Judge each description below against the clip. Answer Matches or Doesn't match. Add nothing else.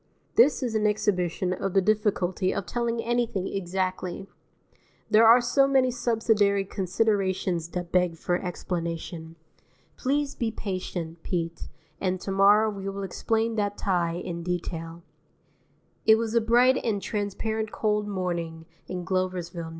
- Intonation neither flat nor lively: Matches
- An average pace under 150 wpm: Matches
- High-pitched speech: Matches